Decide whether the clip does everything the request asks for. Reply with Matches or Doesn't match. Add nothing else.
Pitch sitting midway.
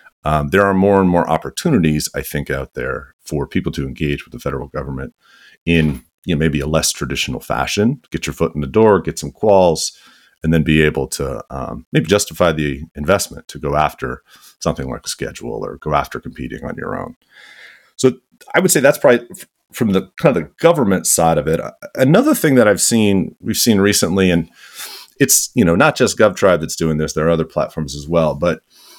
Doesn't match